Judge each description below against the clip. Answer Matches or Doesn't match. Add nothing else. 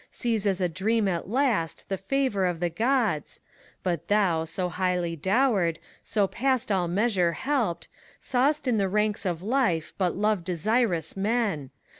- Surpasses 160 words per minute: Doesn't match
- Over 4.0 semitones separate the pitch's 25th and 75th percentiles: Matches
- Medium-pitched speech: Doesn't match